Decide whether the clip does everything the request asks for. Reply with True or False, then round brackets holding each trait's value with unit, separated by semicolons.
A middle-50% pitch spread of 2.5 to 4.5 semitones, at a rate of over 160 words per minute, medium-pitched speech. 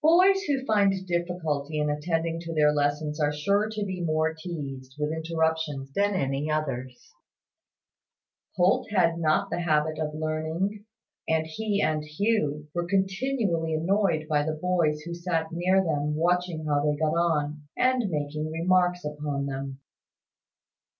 False (3.4 semitones; 145 wpm; 160 Hz)